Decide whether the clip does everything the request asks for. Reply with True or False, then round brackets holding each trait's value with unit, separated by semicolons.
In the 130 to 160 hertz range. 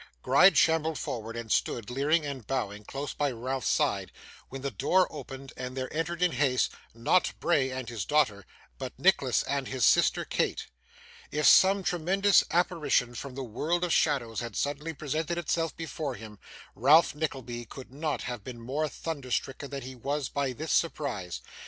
True (140 Hz)